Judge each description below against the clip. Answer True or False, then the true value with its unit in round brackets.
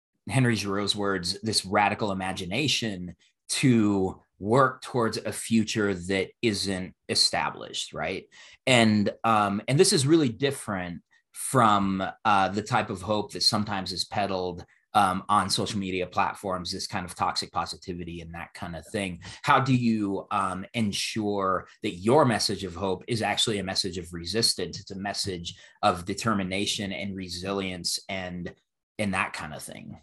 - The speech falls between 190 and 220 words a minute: False (150 wpm)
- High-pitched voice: False (100 Hz)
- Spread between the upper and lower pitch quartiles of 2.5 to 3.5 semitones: True (2.9 semitones)